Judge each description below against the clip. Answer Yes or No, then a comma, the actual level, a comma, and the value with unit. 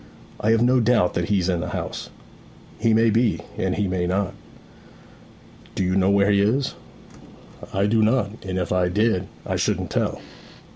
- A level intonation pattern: No, average, 3.4 semitones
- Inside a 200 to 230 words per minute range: No, average, 180 wpm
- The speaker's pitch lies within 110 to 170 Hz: No, low, 100 Hz